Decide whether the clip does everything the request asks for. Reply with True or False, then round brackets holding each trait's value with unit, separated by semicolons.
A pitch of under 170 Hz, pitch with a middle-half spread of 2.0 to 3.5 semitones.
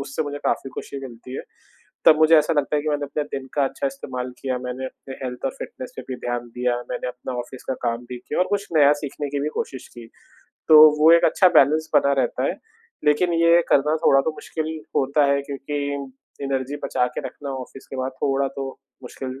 True (140 Hz; 2.7 semitones)